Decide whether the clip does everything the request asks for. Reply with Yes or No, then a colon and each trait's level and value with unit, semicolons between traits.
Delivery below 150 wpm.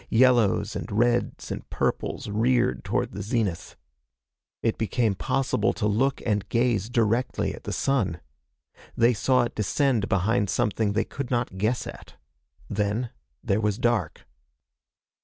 Yes: average, 140 wpm